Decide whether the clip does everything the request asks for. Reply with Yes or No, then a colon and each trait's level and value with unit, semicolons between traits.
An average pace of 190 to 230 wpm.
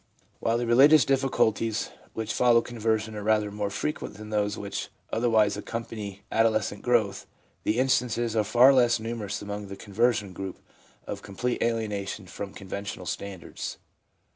No: average, 150 wpm